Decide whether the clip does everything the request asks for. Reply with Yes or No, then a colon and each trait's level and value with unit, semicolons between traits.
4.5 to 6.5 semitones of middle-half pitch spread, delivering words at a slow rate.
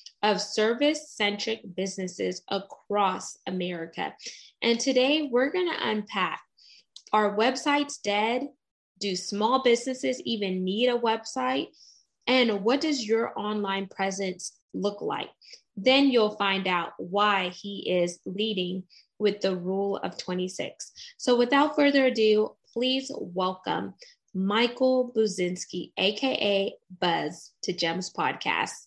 Yes: average, 4.9 semitones; slow, 115 wpm